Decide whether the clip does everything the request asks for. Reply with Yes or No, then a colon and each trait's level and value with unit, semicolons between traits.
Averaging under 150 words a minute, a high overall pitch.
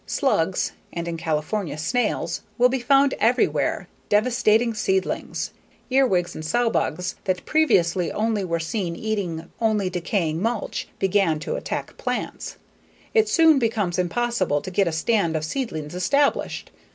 Yes: average, 140 wpm; high, 195 Hz